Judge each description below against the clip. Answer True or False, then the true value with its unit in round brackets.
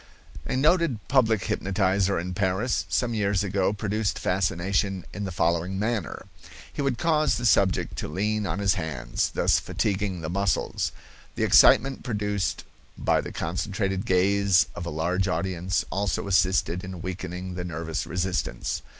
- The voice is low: True (95 Hz)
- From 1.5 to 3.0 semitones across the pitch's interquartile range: True (2.4 semitones)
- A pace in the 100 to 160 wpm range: True (150 wpm)